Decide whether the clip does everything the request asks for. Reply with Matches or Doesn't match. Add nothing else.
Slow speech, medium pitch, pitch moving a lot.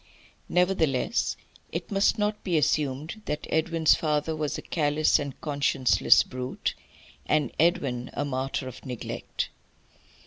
Doesn't match